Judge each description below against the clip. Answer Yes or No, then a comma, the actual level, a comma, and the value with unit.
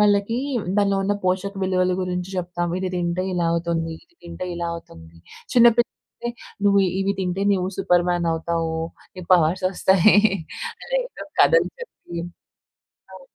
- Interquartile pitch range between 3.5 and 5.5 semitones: No, narrow, 2.5 semitones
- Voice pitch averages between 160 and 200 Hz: Yes, medium, 185 Hz